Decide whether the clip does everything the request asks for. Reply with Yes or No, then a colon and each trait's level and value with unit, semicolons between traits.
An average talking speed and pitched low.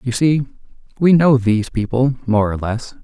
Yes: average, 180 wpm; low, 125 Hz